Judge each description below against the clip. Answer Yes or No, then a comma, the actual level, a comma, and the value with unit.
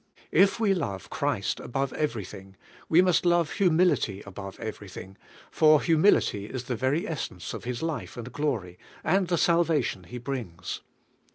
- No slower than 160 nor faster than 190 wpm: No, average, 150 wpm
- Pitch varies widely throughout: Yes, wide, 8.8 semitones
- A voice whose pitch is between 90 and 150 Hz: Yes, low, 135 Hz